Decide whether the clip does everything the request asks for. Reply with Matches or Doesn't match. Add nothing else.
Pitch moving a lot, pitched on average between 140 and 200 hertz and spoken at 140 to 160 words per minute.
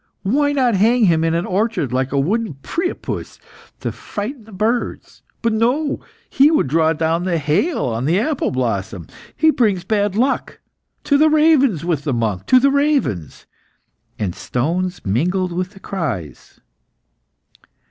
Matches